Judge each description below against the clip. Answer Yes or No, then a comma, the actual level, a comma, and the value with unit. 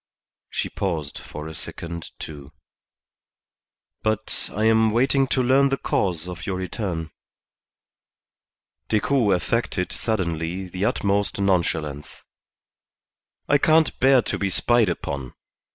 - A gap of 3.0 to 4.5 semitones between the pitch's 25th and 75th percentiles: No, wide, 5.6 semitones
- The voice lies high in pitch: No, very low, 95 Hz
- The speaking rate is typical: No, slow, 115 wpm